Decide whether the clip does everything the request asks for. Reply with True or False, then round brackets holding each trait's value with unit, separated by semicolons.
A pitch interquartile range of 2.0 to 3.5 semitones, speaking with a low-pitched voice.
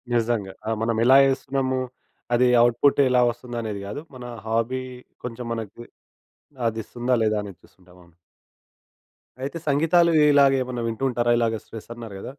True (2.6 semitones; 120 Hz)